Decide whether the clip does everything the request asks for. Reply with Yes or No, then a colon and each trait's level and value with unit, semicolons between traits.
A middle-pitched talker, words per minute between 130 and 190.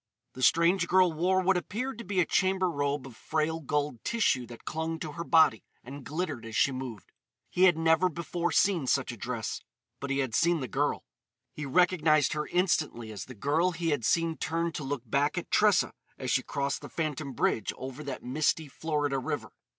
No: medium, 155 Hz; average, 200 wpm